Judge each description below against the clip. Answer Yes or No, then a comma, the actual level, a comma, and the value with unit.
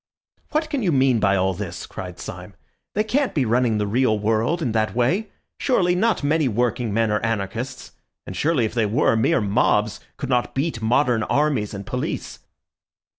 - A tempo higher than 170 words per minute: Yes, average, 180 wpm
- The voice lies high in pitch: No, low, 120 Hz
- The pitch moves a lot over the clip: Yes, wide, 5.8 semitones